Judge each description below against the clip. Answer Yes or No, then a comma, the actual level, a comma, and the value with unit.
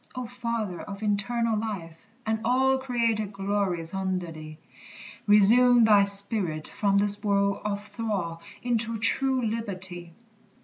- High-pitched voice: Yes, high, 205 Hz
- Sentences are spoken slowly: Yes, slow, 125 wpm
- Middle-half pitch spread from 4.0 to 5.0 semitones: No, average, 3.1 semitones